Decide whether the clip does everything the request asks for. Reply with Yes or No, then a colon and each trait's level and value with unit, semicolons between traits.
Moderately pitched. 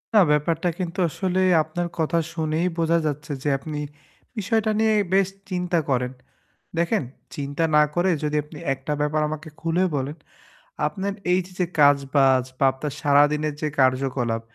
Yes: medium, 155 Hz